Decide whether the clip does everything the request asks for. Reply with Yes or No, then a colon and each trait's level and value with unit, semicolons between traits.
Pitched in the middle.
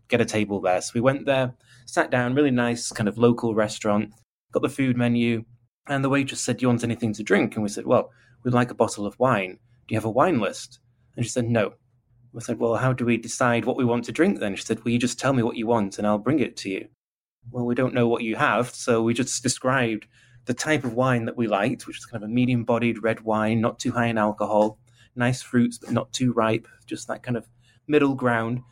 No: low, 120 Hz